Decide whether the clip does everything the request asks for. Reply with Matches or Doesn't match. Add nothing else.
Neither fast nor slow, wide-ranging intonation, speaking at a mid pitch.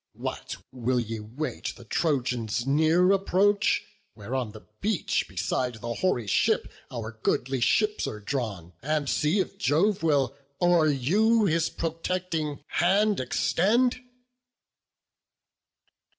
Doesn't match